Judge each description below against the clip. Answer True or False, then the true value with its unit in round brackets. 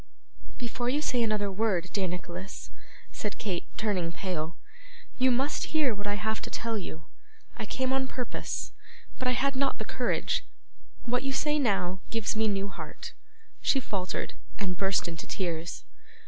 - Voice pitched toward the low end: False (210 Hz)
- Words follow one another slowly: False (160 wpm)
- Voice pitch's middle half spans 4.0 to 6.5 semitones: True (5.2 semitones)